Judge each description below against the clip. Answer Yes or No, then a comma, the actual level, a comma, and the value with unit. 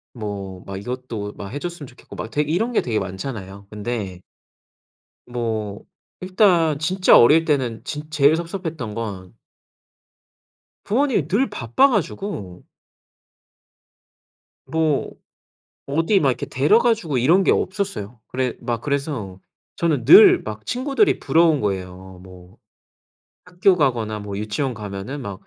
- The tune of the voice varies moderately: No, wide, 8.1 semitones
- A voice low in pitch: Yes, low, 130 Hz